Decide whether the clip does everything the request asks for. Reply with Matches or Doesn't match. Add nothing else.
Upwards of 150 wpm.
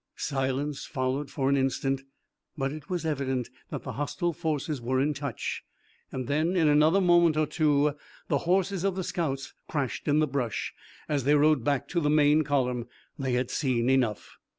Matches